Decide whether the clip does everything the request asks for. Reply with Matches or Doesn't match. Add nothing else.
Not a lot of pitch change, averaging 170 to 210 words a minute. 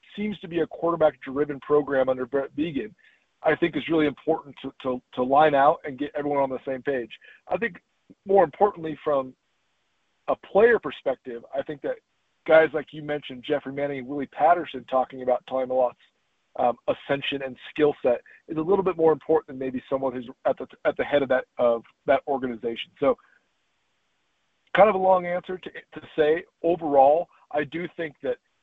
Doesn't match